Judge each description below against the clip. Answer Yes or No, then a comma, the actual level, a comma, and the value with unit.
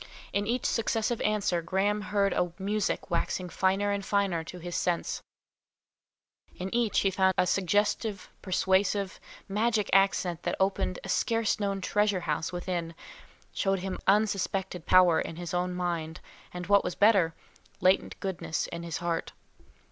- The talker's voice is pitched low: No, high, 190 Hz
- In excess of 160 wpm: No, average, 150 wpm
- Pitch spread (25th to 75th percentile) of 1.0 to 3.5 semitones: Yes, narrow, 2.4 semitones